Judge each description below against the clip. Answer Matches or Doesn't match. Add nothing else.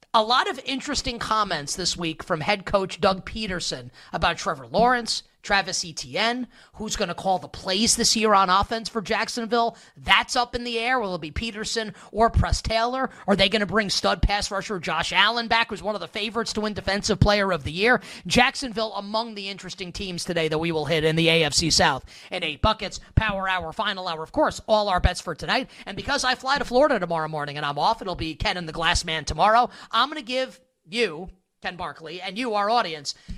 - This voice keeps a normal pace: Doesn't match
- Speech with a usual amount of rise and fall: Matches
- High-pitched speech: Matches